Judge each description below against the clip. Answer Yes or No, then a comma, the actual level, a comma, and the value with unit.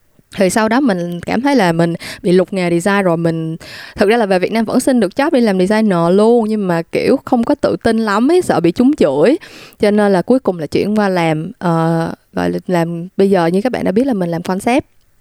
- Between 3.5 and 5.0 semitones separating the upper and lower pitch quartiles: No, wide, 5.5 semitones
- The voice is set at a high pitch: Yes, high, 195 Hz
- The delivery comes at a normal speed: No, fast, 255 wpm